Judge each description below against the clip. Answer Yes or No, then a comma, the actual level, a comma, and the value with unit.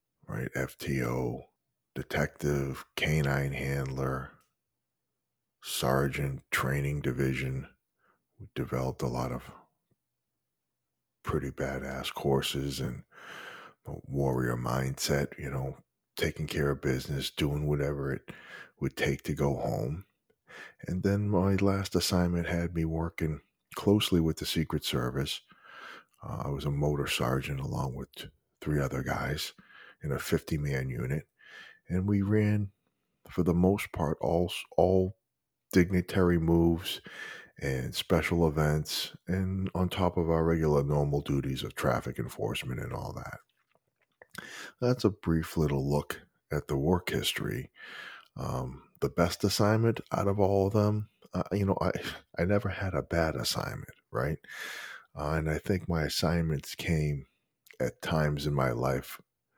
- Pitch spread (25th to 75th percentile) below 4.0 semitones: No, average, 5.0 semitones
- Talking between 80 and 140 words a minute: Yes, slow, 135 wpm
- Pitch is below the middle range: Yes, very low, 75 Hz